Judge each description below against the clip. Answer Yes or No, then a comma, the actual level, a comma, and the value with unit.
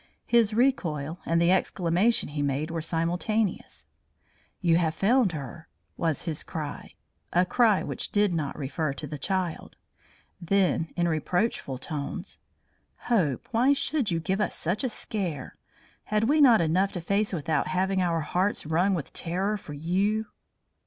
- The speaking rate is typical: Yes, average, 150 wpm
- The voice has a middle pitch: Yes, medium, 175 Hz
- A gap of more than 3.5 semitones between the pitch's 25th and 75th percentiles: Yes, average, 4.5 semitones